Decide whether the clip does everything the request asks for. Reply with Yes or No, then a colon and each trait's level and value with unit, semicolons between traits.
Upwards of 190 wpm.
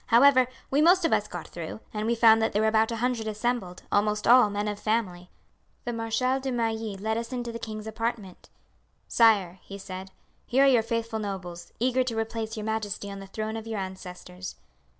Yes: fast, 205 wpm